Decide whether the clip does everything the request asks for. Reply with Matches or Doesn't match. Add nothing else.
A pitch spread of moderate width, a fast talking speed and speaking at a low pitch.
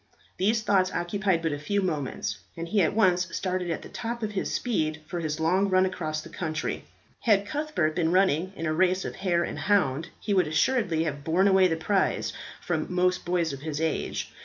Doesn't match